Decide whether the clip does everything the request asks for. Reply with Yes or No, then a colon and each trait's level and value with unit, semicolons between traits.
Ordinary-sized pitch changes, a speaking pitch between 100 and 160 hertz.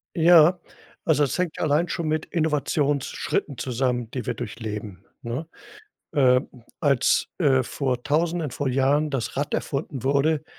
Yes: average, 3.5 semitones; medium, 140 Hz